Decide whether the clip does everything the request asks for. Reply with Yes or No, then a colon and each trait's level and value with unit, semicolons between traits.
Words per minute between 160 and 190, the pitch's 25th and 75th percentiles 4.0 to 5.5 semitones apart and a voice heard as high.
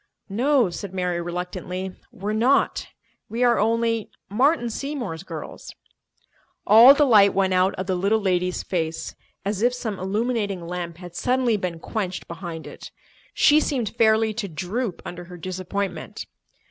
No: average, 145 wpm; average, 4.3 semitones; high, 200 Hz